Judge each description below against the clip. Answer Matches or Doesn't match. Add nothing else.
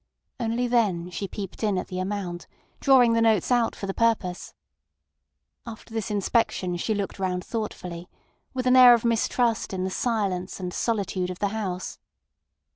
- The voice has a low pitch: Doesn't match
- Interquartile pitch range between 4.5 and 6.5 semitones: Doesn't match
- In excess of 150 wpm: Matches